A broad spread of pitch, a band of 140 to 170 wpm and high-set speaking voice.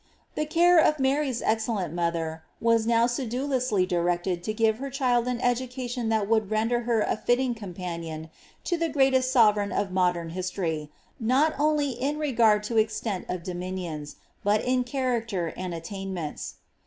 Yes: wide, 5.7 semitones; average, 155 wpm; high, 225 Hz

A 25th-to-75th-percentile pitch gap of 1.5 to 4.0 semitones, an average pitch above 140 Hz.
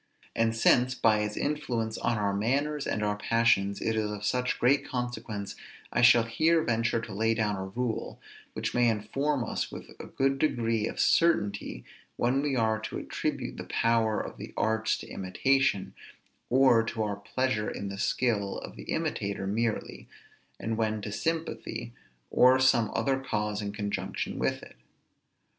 No: average, 3.2 semitones; low, 115 Hz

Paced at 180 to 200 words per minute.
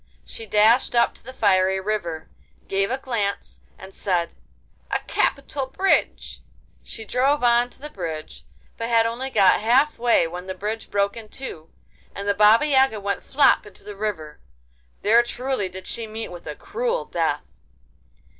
No: average, 165 wpm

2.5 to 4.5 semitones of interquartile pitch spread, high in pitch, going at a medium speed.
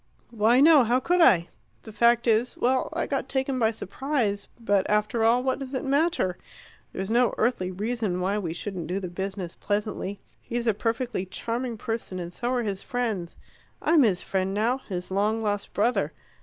Yes: average, 4.1 semitones; high, 225 Hz; average, 185 wpm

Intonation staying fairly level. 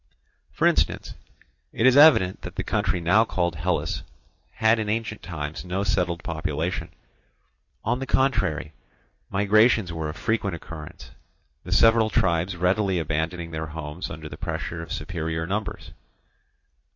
No: average, 4.7 semitones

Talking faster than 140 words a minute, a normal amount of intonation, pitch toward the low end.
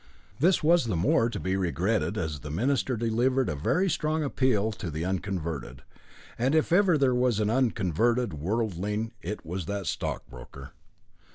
No: average, 160 wpm; wide, 6.3 semitones; low, 110 Hz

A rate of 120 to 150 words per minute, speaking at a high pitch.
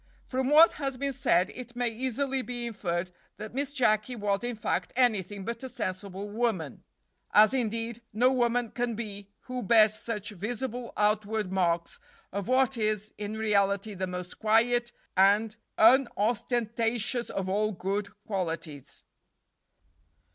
Yes: average, 140 wpm; high, 220 Hz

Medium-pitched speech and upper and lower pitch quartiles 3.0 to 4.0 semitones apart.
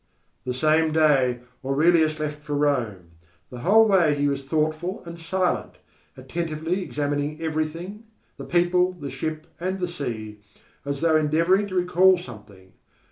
Yes: medium, 155 Hz; average, 3.7 semitones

